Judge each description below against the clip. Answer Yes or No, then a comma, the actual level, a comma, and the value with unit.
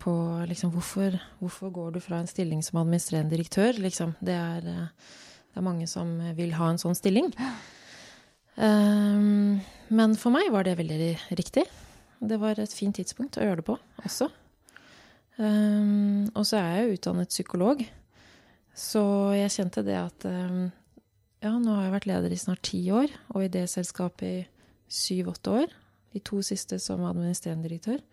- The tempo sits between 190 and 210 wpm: No, average, 170 wpm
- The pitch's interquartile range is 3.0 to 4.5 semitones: Yes, average, 3.6 semitones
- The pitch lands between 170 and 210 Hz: Yes, medium, 185 Hz